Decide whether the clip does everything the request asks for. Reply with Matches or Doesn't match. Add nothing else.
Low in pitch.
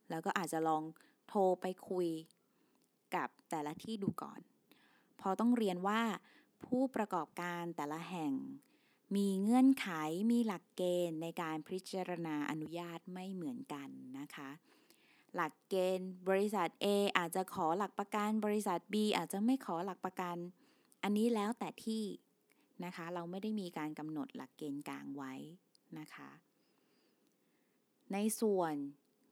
Doesn't match